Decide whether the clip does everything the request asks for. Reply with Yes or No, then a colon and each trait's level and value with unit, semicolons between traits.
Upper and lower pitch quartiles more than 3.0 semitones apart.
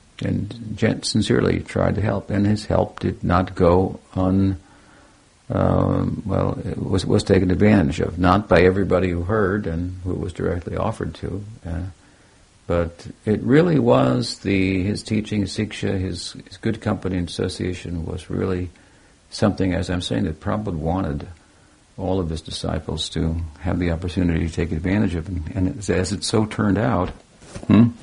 No: average, 2.7 semitones